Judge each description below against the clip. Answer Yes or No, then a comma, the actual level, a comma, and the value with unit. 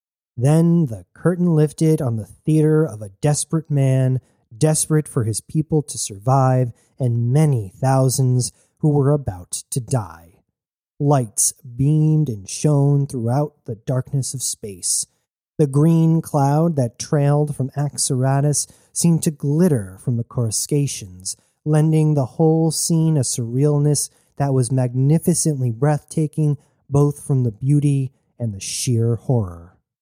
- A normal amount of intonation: Yes, average, 3.9 semitones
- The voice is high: No, medium, 140 Hz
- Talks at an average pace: No, slow, 130 wpm